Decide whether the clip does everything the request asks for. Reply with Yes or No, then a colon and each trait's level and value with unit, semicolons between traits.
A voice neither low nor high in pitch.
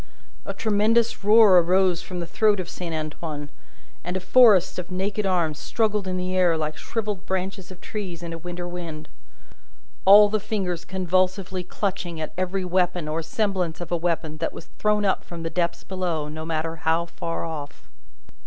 Yes: medium, 180 Hz